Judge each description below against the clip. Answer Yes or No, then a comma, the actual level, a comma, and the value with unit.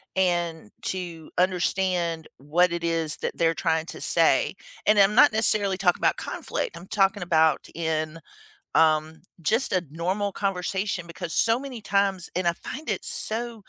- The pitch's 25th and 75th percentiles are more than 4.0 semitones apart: No, average, 3.4 semitones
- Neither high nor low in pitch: Yes, medium, 180 Hz